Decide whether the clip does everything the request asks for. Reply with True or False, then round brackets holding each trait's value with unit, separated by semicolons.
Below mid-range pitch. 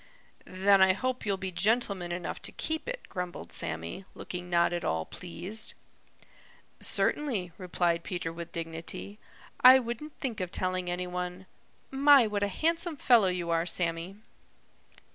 False (185 Hz)